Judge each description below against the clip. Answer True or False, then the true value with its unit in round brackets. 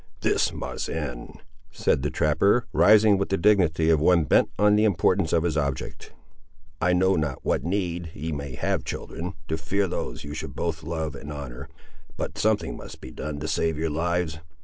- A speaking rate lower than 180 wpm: False (195 wpm)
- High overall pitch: False (80 Hz)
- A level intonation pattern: False (3.3 semitones)